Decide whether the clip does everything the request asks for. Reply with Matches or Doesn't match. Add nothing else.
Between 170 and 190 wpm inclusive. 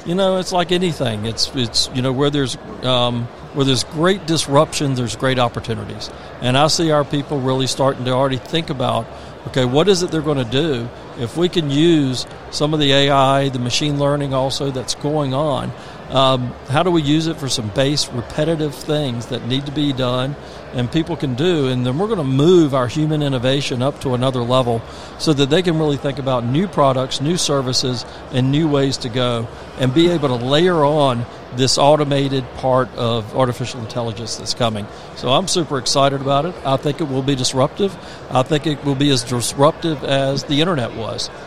Doesn't match